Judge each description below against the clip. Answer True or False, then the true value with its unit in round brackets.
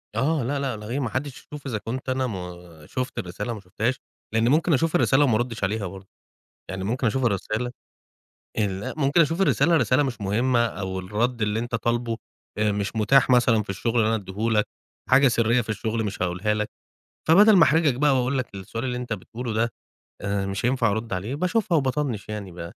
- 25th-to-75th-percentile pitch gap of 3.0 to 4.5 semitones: True (4.0 semitones)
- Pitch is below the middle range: True (115 Hz)